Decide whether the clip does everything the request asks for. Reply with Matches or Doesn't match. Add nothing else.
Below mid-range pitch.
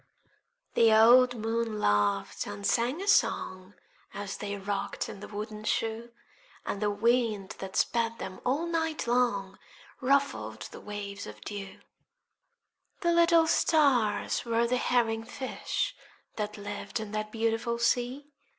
Doesn't match